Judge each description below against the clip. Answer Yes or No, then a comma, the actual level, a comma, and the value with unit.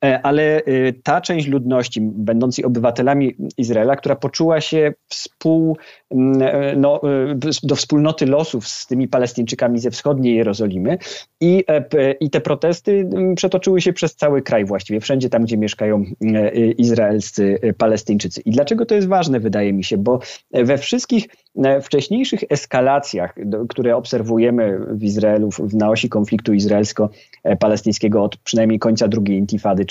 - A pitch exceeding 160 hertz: No, low, 125 Hz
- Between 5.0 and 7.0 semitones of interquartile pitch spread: Yes, average, 5.3 semitones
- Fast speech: No, average, 130 wpm